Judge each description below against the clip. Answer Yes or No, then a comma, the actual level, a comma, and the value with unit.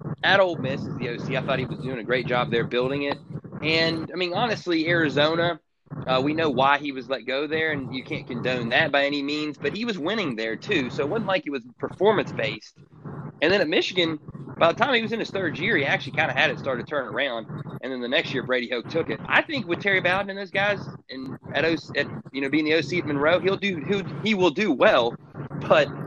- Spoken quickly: Yes, fast, 255 wpm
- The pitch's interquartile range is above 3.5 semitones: Yes, average, 4.5 semitones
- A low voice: No, medium, 155 Hz